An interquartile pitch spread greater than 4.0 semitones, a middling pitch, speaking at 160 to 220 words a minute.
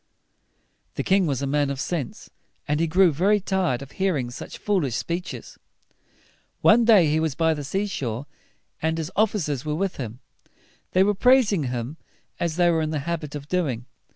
Yes: average, 5.1 semitones; medium, 160 Hz; average, 190 wpm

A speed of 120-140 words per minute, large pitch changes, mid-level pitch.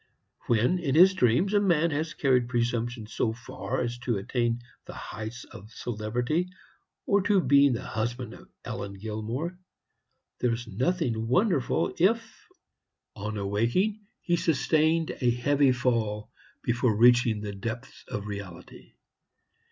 No: slow, 135 wpm; wide, 6.2 semitones; low, 120 Hz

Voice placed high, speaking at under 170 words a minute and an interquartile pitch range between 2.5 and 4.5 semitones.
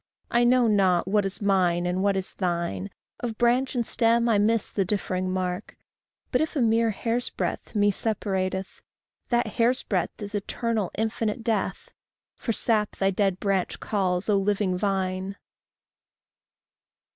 Yes: high, 205 Hz; average, 150 wpm; average, 3.4 semitones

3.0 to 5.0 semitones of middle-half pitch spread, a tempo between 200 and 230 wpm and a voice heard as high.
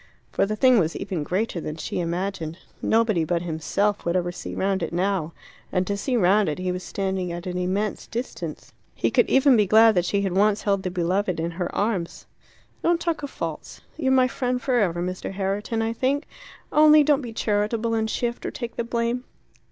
Yes: average, 4.5 semitones; fast, 205 wpm; high, 200 Hz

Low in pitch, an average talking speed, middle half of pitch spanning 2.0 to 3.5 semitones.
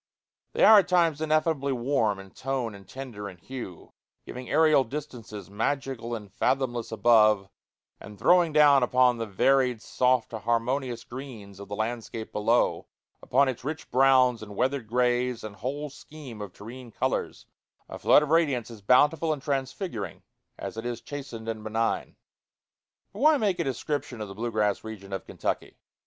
No: low, 125 Hz; average, 165 wpm; average, 4.2 semitones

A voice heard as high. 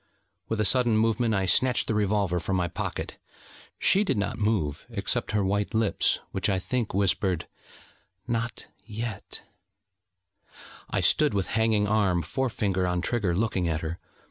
No: low, 105 Hz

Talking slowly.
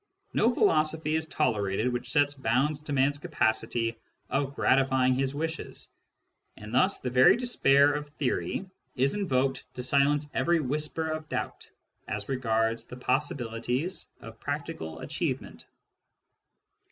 Yes: slow, 130 wpm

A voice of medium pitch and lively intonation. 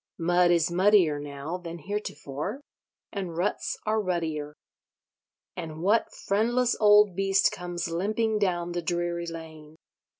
No: medium, 175 Hz; average, 3.9 semitones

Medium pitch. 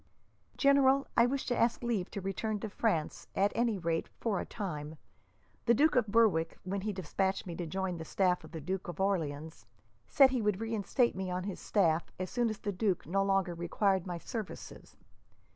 No: high, 195 Hz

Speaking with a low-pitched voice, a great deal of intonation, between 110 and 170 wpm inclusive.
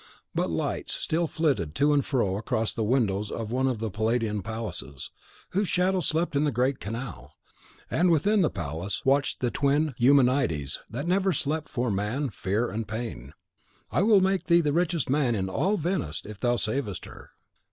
No: low, 125 Hz; wide, 6.7 semitones; average, 180 wpm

